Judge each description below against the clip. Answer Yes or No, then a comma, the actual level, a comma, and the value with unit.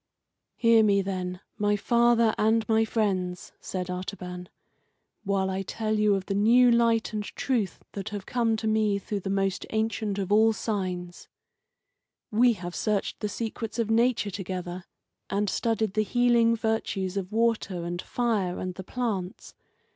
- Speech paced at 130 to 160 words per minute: Yes, average, 145 wpm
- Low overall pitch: No, high, 210 Hz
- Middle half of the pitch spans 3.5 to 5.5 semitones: No, average, 3.0 semitones